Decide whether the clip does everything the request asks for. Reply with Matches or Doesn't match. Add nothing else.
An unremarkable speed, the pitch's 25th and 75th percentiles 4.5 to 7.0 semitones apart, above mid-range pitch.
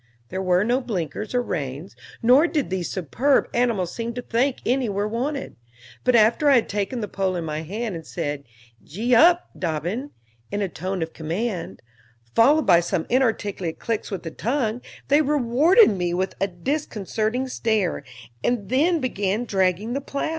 Matches